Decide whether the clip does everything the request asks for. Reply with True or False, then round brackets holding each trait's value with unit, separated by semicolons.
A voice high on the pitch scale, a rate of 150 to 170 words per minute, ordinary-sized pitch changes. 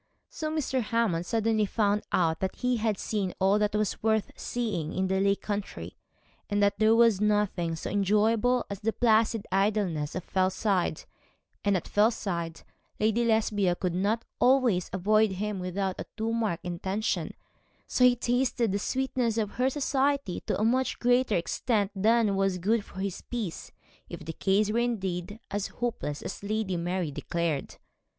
True (210 Hz; 165 wpm; 3.3 semitones)